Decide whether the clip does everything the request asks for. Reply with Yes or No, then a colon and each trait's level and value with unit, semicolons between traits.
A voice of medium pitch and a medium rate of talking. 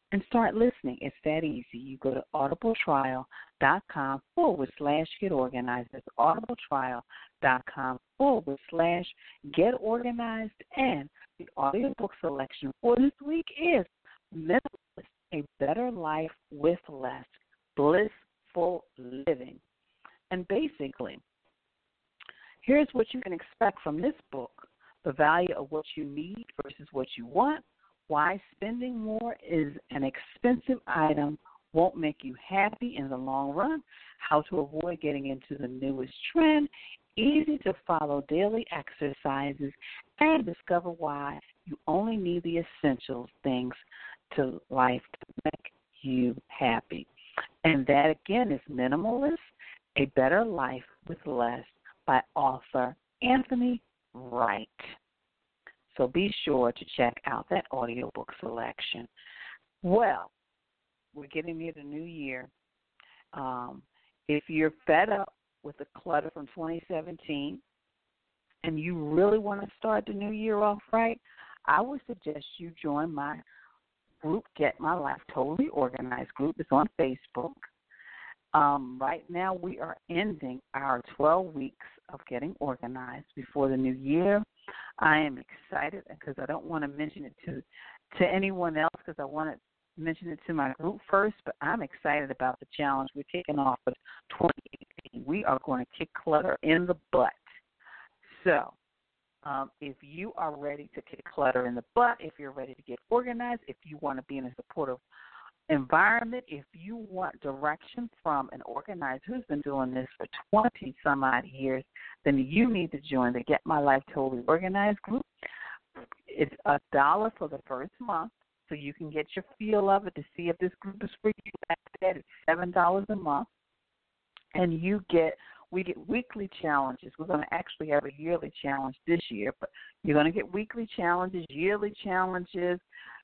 Yes: medium, 155 Hz; average, 150 wpm